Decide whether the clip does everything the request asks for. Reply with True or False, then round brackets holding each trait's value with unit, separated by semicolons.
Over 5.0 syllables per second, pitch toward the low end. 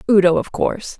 False (6.3 syllables/s; 195 Hz)